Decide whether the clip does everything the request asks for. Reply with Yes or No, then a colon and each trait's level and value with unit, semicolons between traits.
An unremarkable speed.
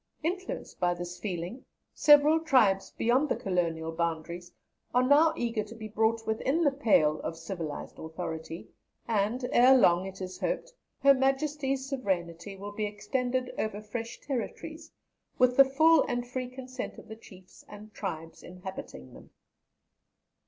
Yes: average, 145 wpm